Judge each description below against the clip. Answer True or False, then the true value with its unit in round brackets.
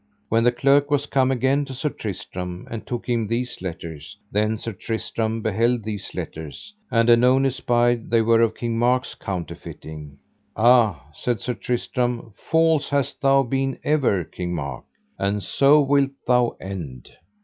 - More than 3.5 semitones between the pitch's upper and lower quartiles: True (4.6 semitones)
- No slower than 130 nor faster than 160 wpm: True (155 wpm)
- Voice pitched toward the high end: False (120 Hz)